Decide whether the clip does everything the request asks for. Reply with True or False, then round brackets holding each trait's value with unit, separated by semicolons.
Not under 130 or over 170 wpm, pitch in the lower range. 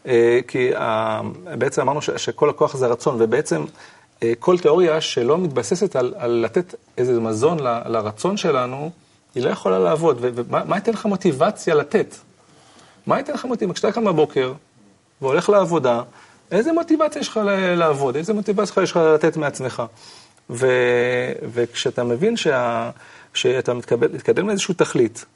False (135 wpm; 155 Hz)